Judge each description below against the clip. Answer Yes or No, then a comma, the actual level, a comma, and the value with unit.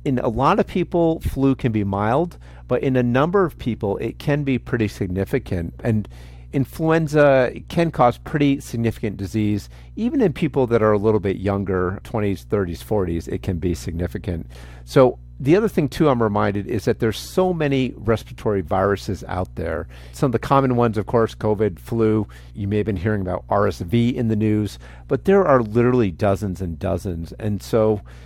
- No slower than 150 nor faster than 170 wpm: No, average, 185 wpm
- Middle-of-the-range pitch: No, low, 110 Hz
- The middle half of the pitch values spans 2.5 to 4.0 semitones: No, average, 5.3 semitones